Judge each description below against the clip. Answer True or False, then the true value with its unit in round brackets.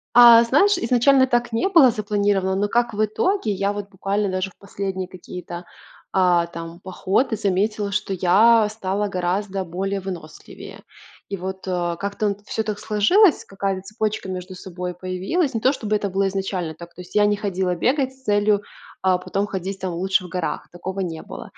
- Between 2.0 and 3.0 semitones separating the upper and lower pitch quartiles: True (2.7 semitones)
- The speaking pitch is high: True (195 Hz)